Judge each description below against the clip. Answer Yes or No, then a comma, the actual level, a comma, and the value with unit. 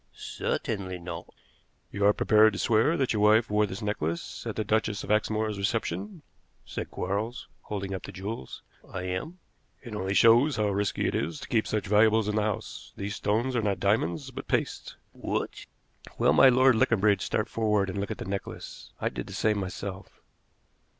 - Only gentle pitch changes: Yes, narrow, 2.2 semitones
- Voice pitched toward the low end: Yes, low, 105 Hz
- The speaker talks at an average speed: Yes, average, 185 wpm